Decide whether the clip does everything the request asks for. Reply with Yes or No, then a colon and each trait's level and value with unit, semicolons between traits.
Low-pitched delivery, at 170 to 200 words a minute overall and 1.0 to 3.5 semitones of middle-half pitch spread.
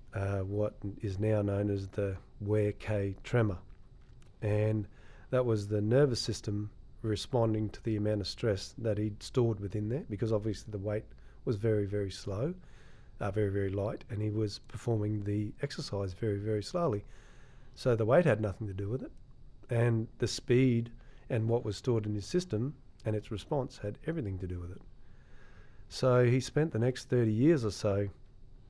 Yes: low, 110 Hz; average, 180 wpm; average, 3.2 semitones